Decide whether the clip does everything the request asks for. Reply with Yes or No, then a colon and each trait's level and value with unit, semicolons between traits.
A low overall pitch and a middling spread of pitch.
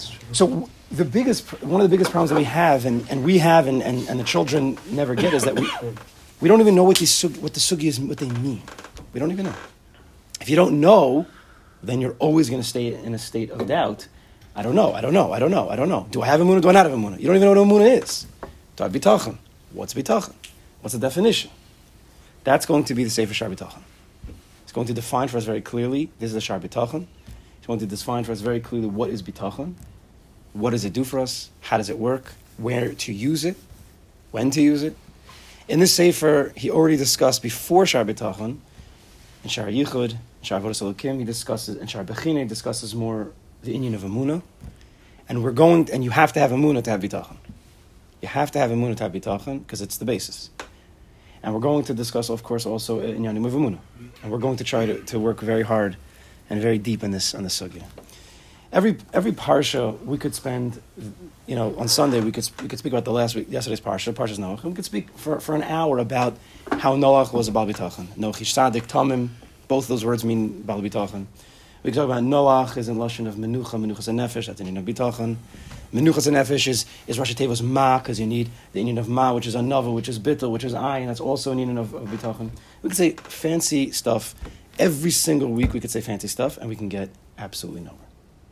Yes: low, 120 Hz; average, 3.9 semitones